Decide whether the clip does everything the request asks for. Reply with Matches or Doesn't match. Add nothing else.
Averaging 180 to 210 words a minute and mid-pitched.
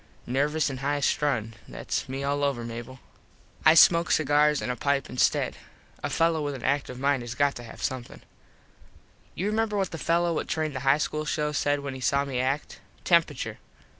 Matches